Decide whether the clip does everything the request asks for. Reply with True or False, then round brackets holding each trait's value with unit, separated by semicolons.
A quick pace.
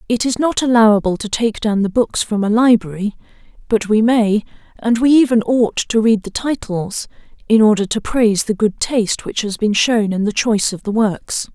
True (210 wpm)